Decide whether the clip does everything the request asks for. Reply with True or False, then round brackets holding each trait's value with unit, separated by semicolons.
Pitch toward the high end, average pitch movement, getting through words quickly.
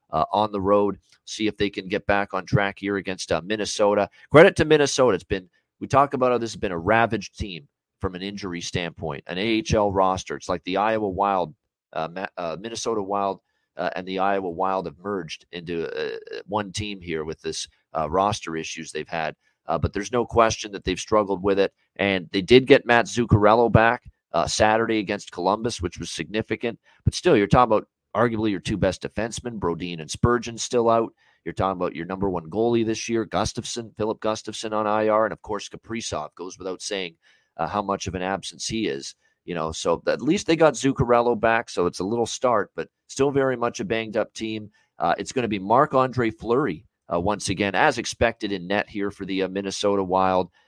False (105 Hz; 3.3 semitones; 210 wpm)